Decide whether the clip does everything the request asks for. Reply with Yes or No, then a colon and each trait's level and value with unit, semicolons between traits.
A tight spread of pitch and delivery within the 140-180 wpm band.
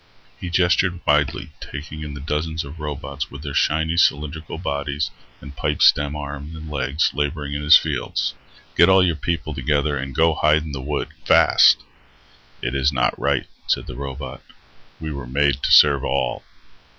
Yes: narrow, 1.8 semitones; average, 170 wpm